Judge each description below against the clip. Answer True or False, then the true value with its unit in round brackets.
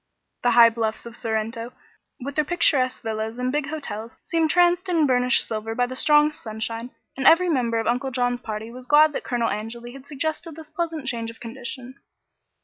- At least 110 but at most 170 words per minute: False (190 wpm)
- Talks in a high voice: True (250 Hz)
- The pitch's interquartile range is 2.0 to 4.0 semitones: False (4.5 semitones)